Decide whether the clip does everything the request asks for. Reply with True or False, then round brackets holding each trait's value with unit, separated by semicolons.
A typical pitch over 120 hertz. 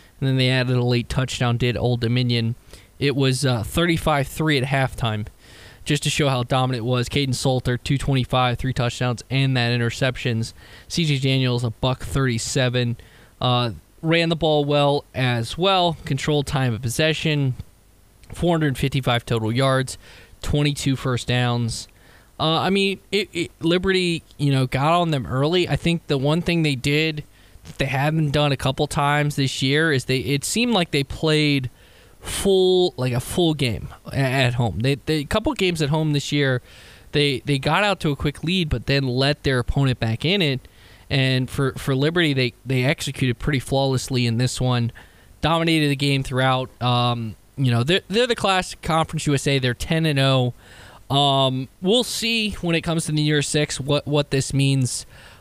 True (135 Hz)